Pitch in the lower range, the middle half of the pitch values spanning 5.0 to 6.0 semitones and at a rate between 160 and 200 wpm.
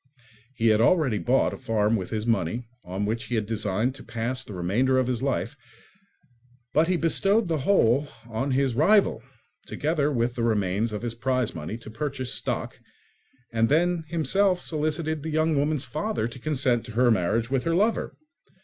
Yes: low, 130 Hz; wide, 5.4 semitones; average, 180 wpm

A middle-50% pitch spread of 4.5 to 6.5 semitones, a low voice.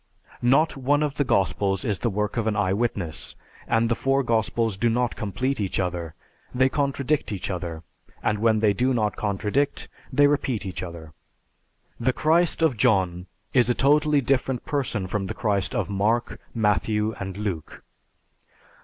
Yes: average, 5.0 semitones; low, 110 Hz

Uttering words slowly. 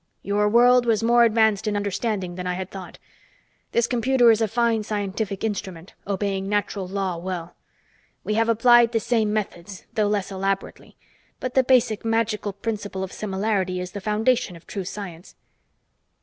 No: average, 165 wpm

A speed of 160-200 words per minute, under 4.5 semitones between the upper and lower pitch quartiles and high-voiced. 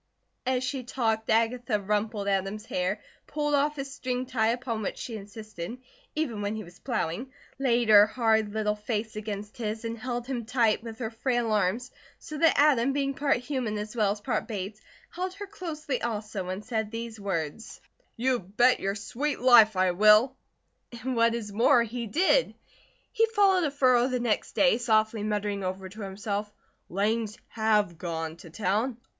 Yes: average, 175 wpm; average, 3.4 semitones; high, 225 Hz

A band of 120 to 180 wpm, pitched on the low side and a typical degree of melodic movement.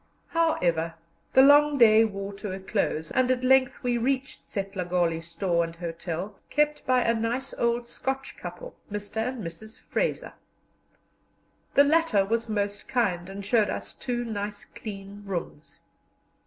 No: average, 145 wpm; high, 215 Hz; average, 4.8 semitones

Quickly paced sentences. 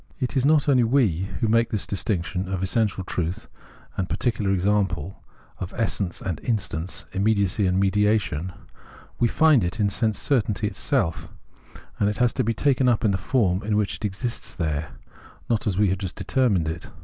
No: average, 180 wpm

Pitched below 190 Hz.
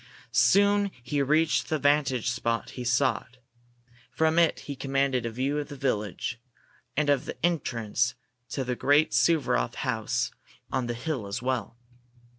Yes: low, 135 Hz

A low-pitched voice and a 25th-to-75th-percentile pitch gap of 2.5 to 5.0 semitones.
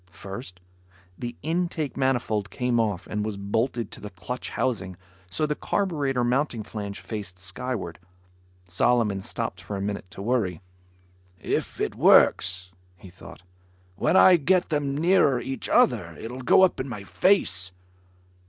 No: low, 115 Hz; wide, 5.6 semitones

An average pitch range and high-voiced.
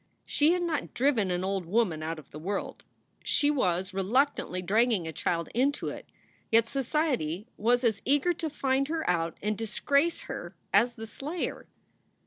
No: wide, 7.4 semitones; high, 225 Hz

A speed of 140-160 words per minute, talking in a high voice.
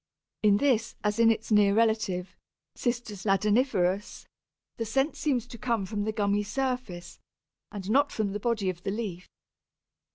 Yes: average, 155 wpm; high, 215 Hz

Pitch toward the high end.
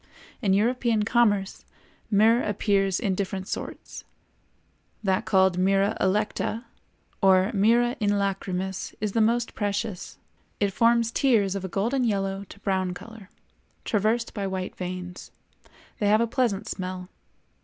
Yes: high, 200 Hz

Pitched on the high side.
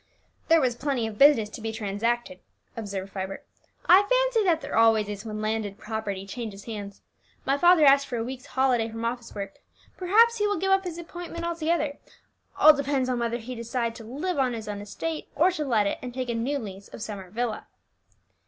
Yes: high, 240 Hz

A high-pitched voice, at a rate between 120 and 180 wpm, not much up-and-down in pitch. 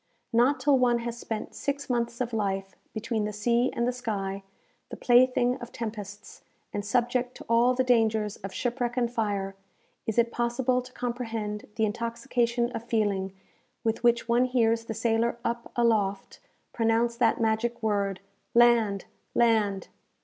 Yes: high, 235 Hz; average, 155 wpm; narrow, 2.1 semitones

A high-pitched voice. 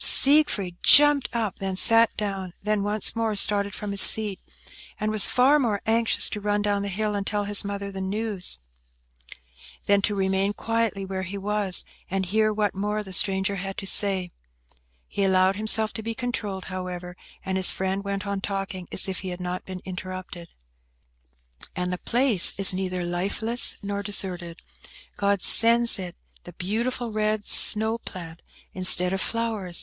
Yes: high, 200 Hz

